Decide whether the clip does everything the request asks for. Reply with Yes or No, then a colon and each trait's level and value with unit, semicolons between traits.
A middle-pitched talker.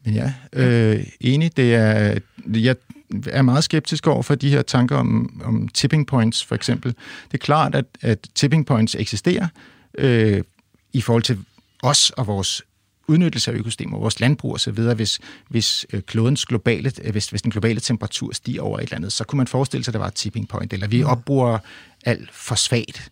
No: low, 120 Hz